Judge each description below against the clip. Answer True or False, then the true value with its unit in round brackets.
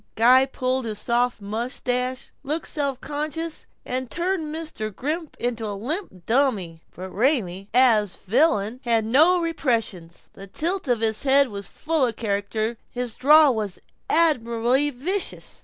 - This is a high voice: True (250 Hz)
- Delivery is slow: False (145 wpm)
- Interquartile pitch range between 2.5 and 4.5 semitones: False (5.3 semitones)